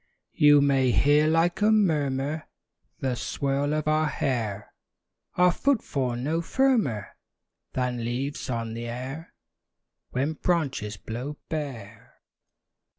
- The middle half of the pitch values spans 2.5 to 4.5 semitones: Yes, average, 4.1 semitones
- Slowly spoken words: Yes, slow, 110 wpm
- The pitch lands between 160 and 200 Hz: No, medium, 140 Hz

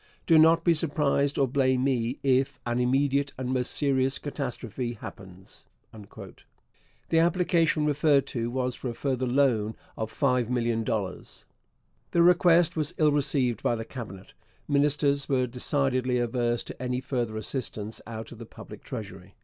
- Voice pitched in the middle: No, low, 130 Hz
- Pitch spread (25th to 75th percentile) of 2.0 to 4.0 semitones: Yes, average, 3.3 semitones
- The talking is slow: No, average, 145 wpm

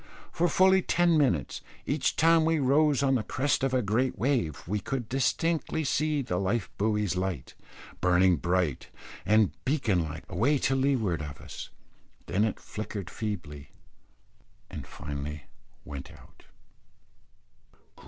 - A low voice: Yes, low, 110 Hz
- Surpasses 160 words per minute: No, slow, 135 wpm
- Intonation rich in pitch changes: Yes, wide, 7.8 semitones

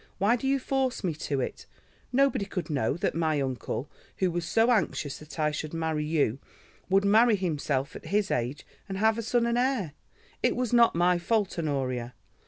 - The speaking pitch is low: No, medium, 175 Hz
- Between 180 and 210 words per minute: Yes, average, 190 wpm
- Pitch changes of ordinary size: No, wide, 7.0 semitones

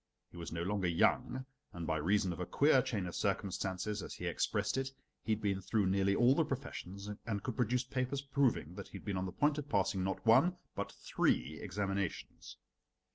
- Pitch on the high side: No, low, 100 Hz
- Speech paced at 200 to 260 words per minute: Yes, fast, 205 wpm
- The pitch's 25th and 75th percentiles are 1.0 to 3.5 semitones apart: No, average, 5.3 semitones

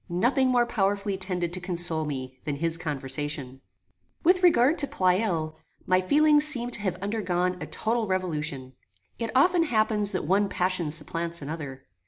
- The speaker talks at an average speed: Yes, average, 155 wpm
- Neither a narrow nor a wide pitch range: No, wide, 6.1 semitones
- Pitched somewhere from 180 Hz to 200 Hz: Yes, medium, 185 Hz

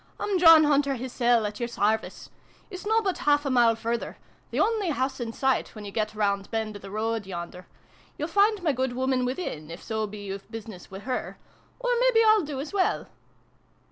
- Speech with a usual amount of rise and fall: No, wide, 6.6 semitones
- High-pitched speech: Yes, high, 245 Hz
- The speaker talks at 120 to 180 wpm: No, fast, 205 wpm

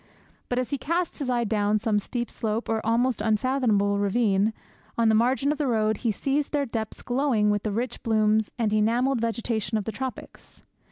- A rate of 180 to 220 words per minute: Yes, average, 190 wpm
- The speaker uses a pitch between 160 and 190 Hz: No, high, 225 Hz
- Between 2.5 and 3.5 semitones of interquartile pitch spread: Yes, average, 2.9 semitones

